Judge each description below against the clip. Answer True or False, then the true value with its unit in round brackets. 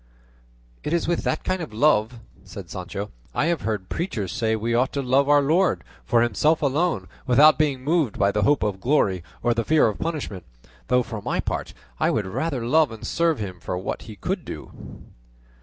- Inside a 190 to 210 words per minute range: True (200 wpm)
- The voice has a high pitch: False (125 Hz)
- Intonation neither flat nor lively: False (6.5 semitones)